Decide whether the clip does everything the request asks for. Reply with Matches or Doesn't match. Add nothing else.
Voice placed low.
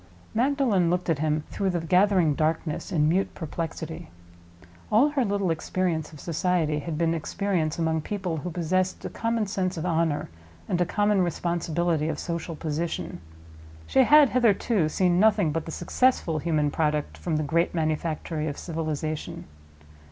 Doesn't match